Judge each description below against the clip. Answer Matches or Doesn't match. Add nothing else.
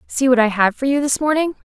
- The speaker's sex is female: Matches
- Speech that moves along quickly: Matches